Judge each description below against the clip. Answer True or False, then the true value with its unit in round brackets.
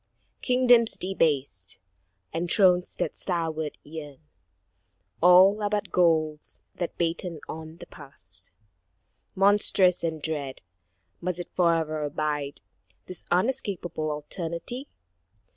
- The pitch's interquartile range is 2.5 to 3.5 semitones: True (3.1 semitones)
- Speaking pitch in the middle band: True (170 Hz)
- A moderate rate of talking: False (100 wpm)